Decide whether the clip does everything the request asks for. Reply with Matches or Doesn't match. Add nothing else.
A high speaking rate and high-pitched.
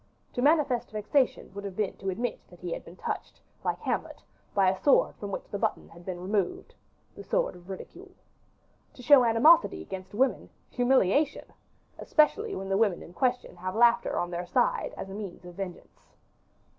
Doesn't match